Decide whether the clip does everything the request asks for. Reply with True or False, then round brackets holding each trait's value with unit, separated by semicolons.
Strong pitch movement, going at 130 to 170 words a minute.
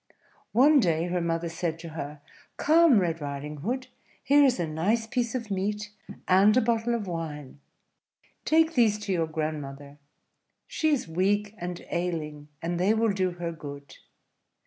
True (6.0 semitones; 160 wpm)